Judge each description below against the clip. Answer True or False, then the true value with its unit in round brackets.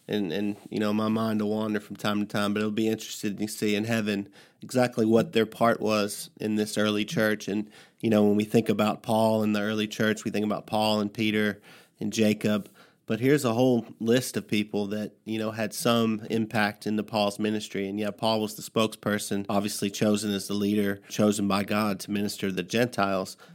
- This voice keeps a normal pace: False (210 wpm)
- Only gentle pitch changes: True (1.2 semitones)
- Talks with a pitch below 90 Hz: False (105 Hz)